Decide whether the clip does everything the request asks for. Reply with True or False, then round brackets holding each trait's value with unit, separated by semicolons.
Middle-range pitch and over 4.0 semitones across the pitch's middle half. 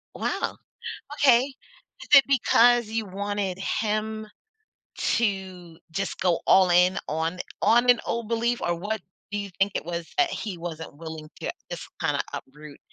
False (200 Hz; 5.0 semitones)